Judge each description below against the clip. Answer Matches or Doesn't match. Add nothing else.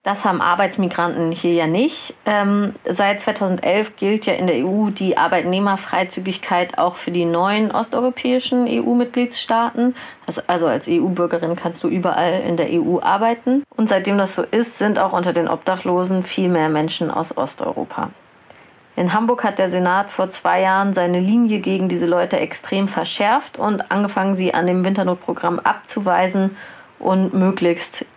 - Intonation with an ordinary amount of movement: Matches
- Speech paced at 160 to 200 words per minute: Doesn't match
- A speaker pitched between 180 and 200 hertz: Matches